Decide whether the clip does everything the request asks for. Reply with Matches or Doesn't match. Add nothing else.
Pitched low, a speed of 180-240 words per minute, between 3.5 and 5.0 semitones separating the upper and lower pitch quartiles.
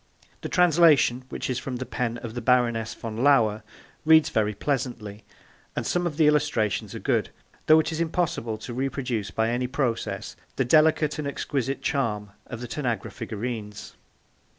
Doesn't match